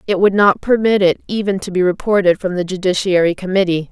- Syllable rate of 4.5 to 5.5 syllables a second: No, 6.0 syllables/s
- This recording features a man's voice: No, female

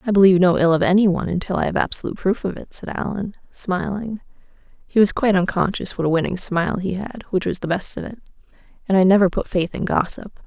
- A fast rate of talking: Yes, fast, 210 wpm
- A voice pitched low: No, high, 190 Hz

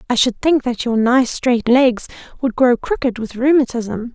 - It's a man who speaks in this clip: No, female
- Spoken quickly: No, average, 190 wpm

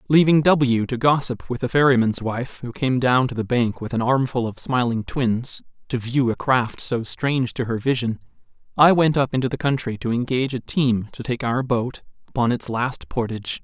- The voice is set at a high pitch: No, low, 125 Hz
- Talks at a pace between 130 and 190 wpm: No, fast, 205 wpm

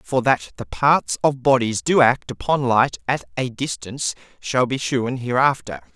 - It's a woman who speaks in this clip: No, male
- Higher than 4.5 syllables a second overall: No, 4.4 syllables/s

